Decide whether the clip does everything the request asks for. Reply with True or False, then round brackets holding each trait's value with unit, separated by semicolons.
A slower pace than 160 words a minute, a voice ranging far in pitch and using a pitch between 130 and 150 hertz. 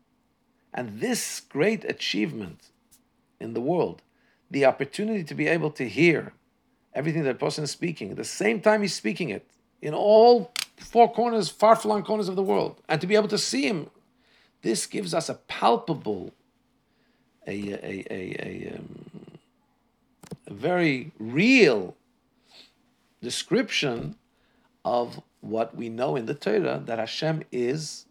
False (140 wpm; 7.0 semitones; 175 Hz)